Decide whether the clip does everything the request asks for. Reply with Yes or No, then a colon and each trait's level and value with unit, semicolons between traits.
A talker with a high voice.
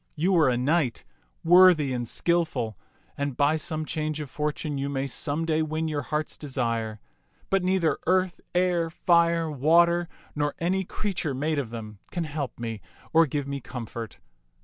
No: medium, 150 Hz